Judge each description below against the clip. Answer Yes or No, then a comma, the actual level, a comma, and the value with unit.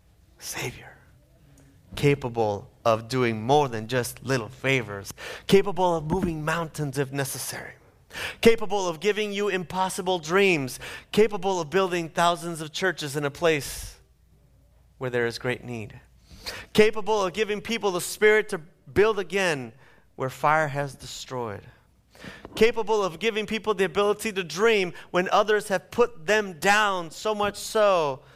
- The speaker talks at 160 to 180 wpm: No, average, 140 wpm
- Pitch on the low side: No, medium, 175 Hz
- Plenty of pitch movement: Yes, wide, 7.3 semitones